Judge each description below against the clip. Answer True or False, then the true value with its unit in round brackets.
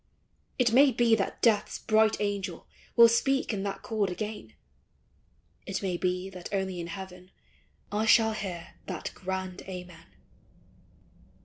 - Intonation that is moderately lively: True (3.3 semitones)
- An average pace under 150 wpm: True (135 wpm)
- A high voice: True (195 Hz)